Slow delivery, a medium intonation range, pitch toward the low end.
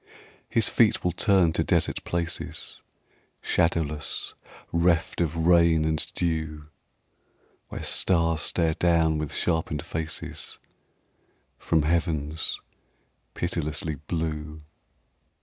No: slow, 95 wpm; narrow, 1.7 semitones; very low, 80 Hz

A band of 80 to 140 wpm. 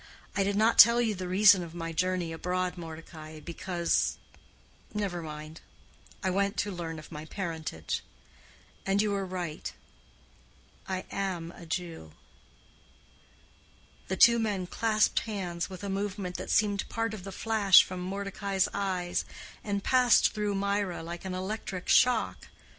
Yes: slow, 135 wpm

